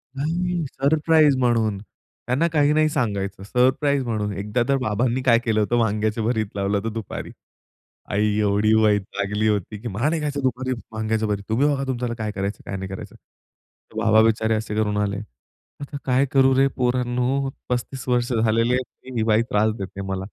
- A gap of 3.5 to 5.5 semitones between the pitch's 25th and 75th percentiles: Yes, average, 3.8 semitones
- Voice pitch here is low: Yes, low, 115 Hz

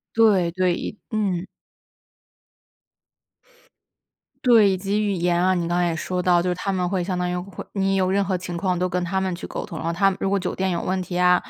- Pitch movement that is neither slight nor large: No, narrow, 1.5 semitones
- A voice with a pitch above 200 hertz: No, medium, 185 Hz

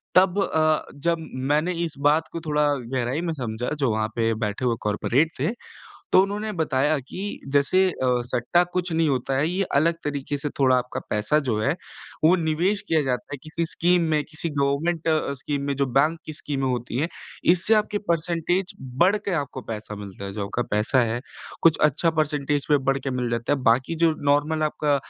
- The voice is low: No, medium, 150 Hz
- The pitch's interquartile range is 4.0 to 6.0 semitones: Yes, average, 4.3 semitones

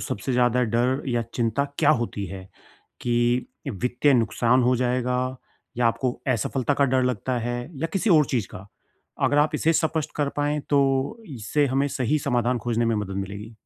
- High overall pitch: No, low, 125 Hz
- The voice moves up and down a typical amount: Yes, average, 3.0 semitones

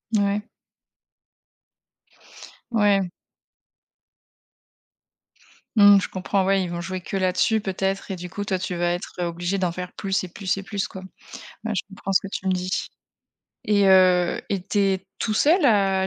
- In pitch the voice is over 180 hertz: Yes, high, 190 Hz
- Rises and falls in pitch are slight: Yes, narrow, 1.7 semitones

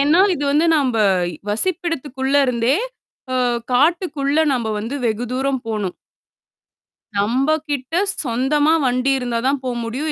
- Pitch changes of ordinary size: Yes, average, 3.5 semitones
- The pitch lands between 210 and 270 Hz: Yes, very high, 265 Hz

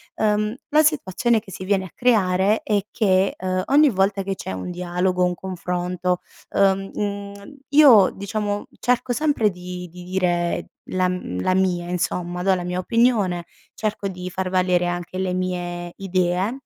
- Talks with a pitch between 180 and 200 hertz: Yes, medium, 185 Hz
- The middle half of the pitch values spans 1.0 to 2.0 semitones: No, narrow, 2.5 semitones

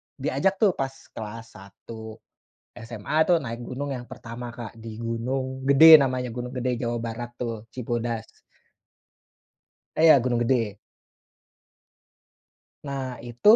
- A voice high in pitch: No, low, 120 Hz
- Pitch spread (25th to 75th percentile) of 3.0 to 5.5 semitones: No, narrow, 2.4 semitones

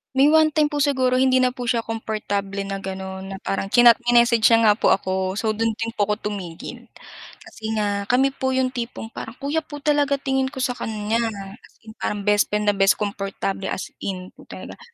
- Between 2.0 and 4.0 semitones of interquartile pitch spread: No, average, 4.5 semitones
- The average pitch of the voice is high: Yes, high, 225 Hz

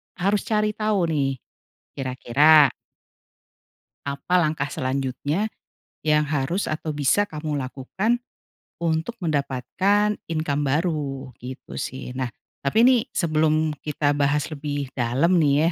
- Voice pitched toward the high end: No, medium, 150 Hz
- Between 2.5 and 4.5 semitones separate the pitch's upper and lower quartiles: Yes, average, 3.8 semitones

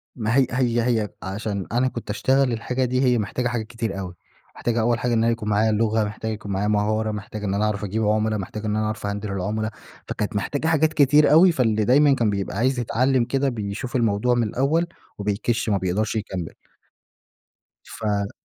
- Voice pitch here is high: No, low, 110 Hz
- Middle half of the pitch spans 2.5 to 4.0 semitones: Yes, average, 3.1 semitones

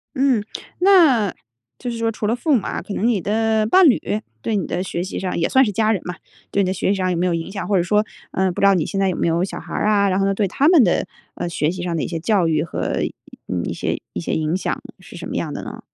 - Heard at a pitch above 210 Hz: No, high, 195 Hz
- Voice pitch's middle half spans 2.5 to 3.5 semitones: No, average, 4.0 semitones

